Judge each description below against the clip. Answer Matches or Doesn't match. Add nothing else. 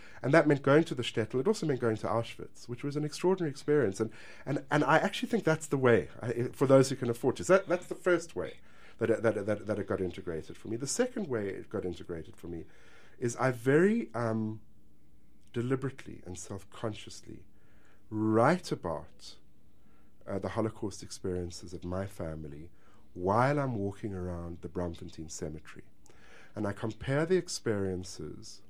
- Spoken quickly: Doesn't match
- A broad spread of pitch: Matches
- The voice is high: Doesn't match